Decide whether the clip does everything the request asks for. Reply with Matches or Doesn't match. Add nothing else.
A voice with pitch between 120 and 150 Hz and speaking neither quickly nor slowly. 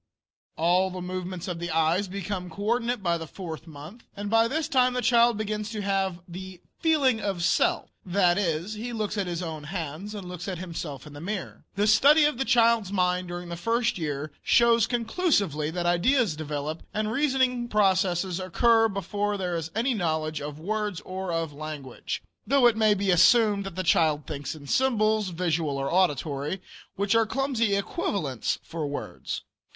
Doesn't match